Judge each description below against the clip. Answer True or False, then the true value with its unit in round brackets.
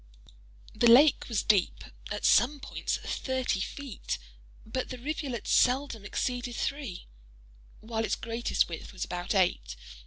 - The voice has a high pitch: True (230 Hz)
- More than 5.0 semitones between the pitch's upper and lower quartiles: True (5.6 semitones)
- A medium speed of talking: False (120 wpm)